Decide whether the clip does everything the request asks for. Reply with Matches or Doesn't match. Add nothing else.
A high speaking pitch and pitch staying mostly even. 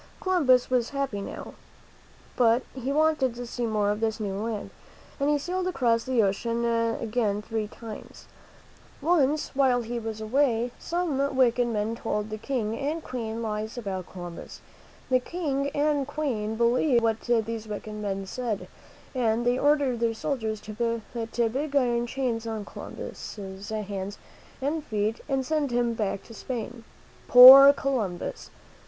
Doesn't match